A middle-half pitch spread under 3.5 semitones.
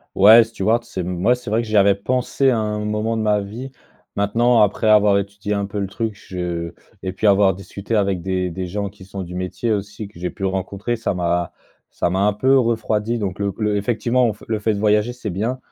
Yes: narrow, 2.6 semitones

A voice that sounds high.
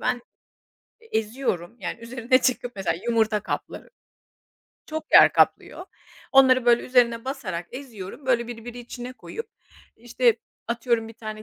Yes: high, 240 Hz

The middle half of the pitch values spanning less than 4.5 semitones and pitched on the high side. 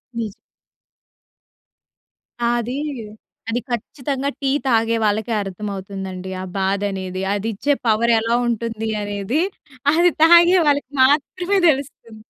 No: wide, 5.4 semitones; high, 230 Hz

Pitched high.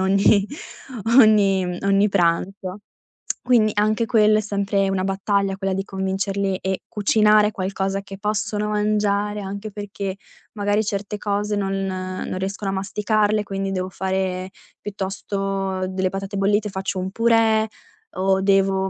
Yes: high, 195 Hz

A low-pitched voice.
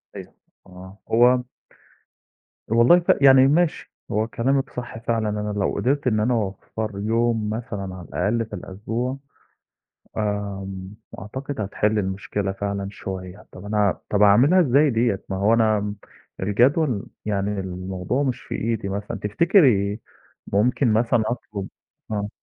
Yes: low, 105 Hz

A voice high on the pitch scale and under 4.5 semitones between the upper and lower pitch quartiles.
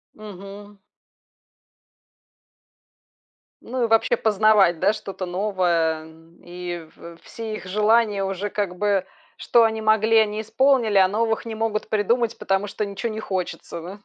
Yes: high, 205 Hz; average, 3.0 semitones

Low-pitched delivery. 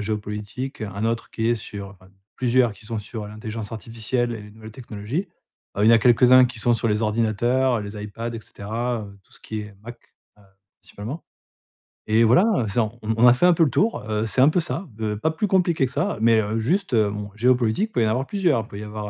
Yes: low, 115 Hz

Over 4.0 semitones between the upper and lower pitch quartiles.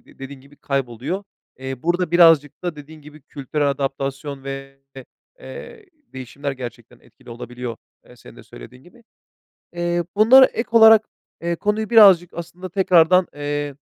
Yes: average, 4.9 semitones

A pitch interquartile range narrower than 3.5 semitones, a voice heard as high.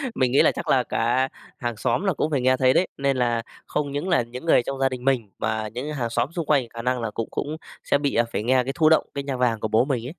No: average, 3.0 semitones; low, 130 Hz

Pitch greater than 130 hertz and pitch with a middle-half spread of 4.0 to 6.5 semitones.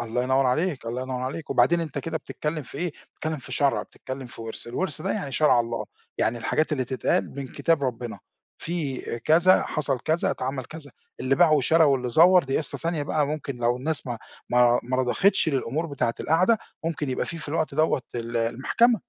Yes: medium, 140 Hz; average, 4.3 semitones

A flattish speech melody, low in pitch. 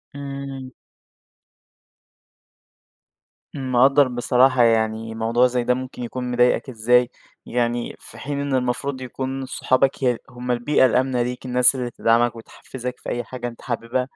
Yes: narrow, 1.4 semitones; low, 125 Hz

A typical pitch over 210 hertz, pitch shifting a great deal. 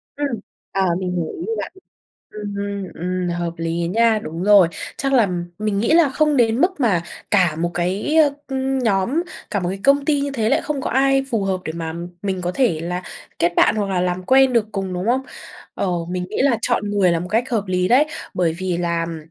No: high, 200 Hz; wide, 6.7 semitones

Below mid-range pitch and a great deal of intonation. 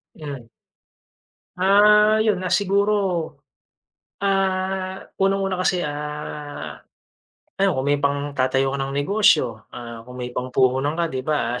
No: medium, 150 Hz; wide, 6.3 semitones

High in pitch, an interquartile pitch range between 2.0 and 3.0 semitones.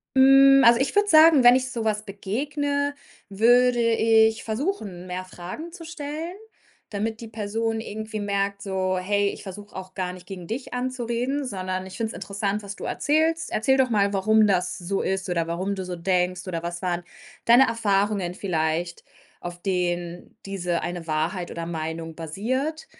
No: high, 205 Hz; average, 5.2 semitones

